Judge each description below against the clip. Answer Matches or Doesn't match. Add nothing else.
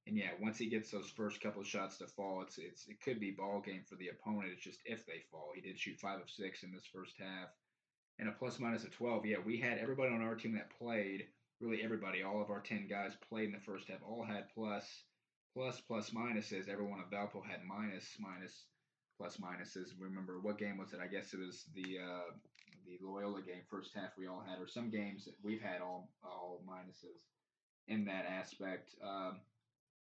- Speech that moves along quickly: Matches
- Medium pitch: Doesn't match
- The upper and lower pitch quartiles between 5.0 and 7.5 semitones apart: Doesn't match